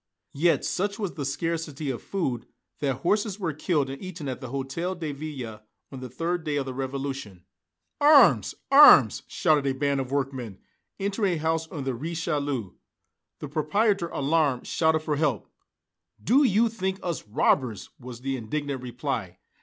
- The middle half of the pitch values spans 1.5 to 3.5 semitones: No, average, 4.4 semitones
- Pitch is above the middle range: No, medium, 145 Hz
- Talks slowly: No, average, 165 wpm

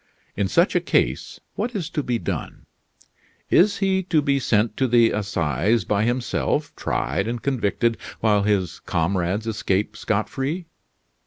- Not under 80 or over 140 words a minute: No, average, 150 wpm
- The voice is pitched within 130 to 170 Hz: No, low, 115 Hz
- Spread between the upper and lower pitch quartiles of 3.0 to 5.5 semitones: Yes, average, 5.2 semitones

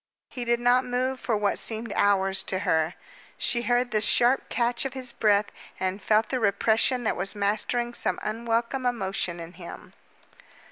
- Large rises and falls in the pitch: No, average, 3.4 semitones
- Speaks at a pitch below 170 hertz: No, high, 225 Hz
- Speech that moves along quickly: No, average, 170 wpm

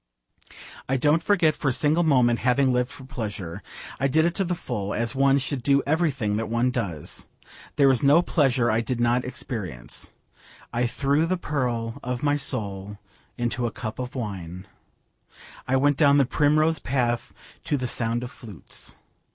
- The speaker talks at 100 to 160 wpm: No, average, 175 wpm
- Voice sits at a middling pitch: No, low, 125 Hz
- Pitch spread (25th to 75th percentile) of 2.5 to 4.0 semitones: Yes, average, 3.6 semitones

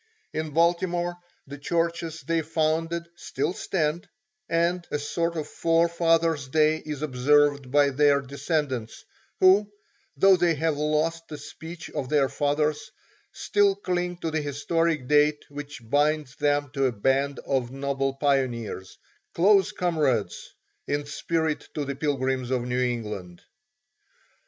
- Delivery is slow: Yes, slow, 130 wpm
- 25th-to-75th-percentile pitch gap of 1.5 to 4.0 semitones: Yes, average, 3.2 semitones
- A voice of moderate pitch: Yes, medium, 150 Hz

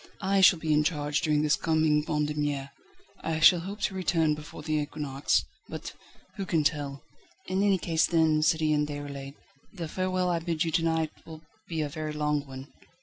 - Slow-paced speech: No, average, 185 wpm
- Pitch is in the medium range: Yes, medium, 155 Hz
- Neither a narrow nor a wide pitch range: No, narrow, 2.0 semitones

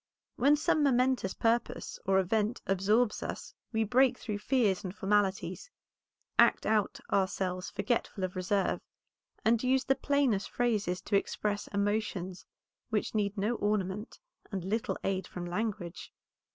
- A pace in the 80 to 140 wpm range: Yes, slow, 135 wpm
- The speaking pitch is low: No, high, 210 Hz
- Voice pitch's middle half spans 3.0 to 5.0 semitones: Yes, average, 3.5 semitones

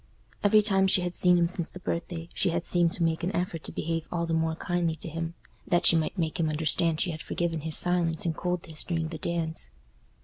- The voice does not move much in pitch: Yes, narrow, 1.5 semitones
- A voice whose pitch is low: No, medium, 170 Hz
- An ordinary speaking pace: No, fast, 235 wpm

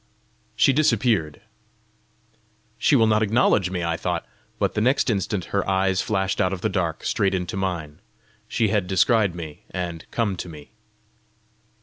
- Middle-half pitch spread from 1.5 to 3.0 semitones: No, average, 3.5 semitones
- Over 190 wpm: No, average, 155 wpm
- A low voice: Yes, very low, 95 Hz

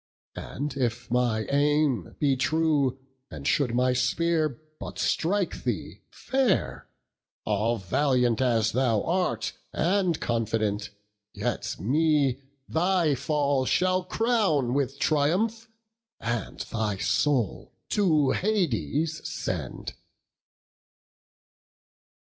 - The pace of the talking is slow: Yes, slow, 95 wpm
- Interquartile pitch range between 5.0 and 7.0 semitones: Yes, wide, 5.4 semitones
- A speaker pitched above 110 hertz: Yes, medium, 140 Hz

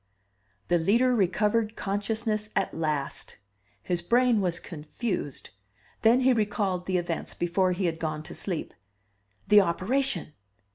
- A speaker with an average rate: No, slow, 130 wpm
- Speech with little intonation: No, average, 4.5 semitones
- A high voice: Yes, high, 195 Hz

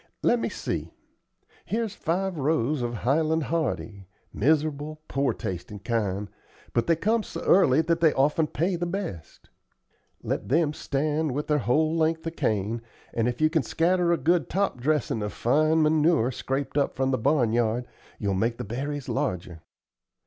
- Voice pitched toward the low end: No, medium, 145 Hz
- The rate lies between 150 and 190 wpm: Yes, average, 165 wpm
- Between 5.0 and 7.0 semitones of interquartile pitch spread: Yes, average, 5.3 semitones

